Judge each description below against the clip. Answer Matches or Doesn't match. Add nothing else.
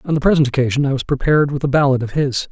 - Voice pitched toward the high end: Doesn't match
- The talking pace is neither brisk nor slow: Doesn't match